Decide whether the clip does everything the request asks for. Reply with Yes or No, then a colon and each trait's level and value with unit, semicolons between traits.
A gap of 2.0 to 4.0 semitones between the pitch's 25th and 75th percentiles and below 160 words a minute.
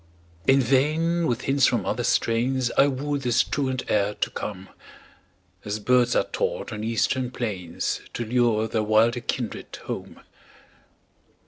Yes: average, 3.5 semitones; average, 140 wpm